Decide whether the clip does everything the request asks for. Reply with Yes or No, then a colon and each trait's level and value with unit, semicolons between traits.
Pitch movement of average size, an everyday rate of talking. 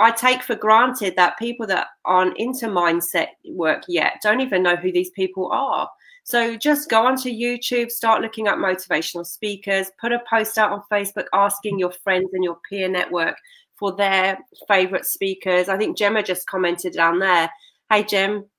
Yes: average, 3.5 semitones; average, 180 wpm